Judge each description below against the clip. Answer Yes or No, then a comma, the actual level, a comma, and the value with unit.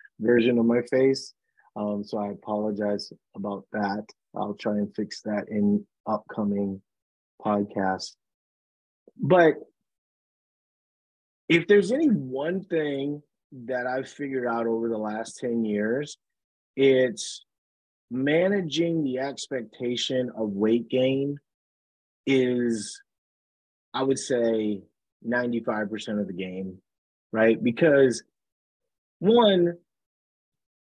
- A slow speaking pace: Yes, slow, 105 wpm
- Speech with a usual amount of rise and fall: Yes, average, 4.7 semitones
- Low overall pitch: Yes, low, 120 Hz